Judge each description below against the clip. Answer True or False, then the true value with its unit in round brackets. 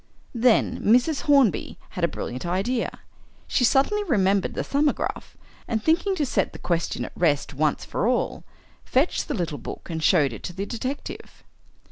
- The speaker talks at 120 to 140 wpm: False (165 wpm)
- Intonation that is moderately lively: False (7.9 semitones)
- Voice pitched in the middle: False (220 Hz)